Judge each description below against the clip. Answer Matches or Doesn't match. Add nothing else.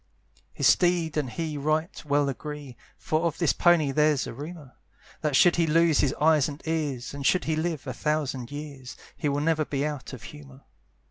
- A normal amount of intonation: Doesn't match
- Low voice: Doesn't match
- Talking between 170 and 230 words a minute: Matches